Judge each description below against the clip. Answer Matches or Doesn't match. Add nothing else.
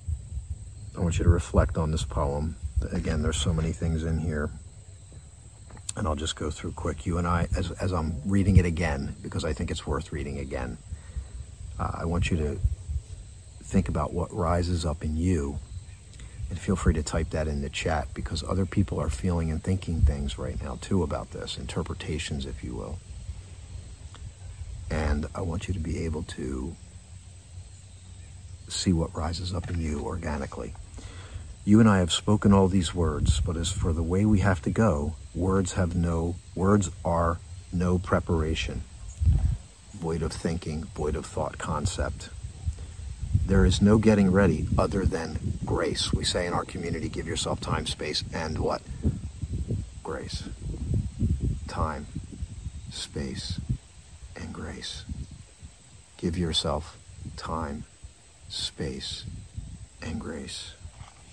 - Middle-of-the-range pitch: Doesn't match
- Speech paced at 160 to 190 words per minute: Doesn't match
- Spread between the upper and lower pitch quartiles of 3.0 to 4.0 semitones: Doesn't match